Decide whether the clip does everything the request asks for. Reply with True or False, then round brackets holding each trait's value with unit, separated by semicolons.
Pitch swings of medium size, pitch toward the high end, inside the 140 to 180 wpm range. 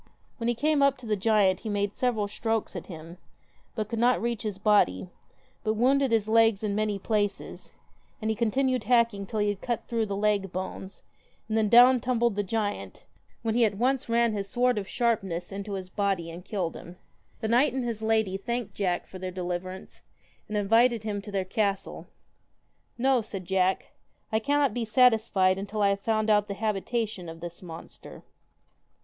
False (3.1 semitones; 215 Hz; 195 wpm)